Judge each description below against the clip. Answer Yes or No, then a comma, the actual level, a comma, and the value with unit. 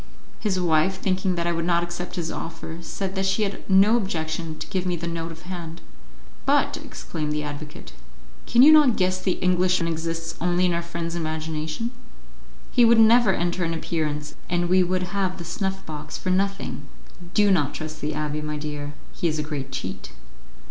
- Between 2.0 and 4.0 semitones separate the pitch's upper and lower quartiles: Yes, average, 3.0 semitones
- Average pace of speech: Yes, average, 190 wpm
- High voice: No, medium, 170 Hz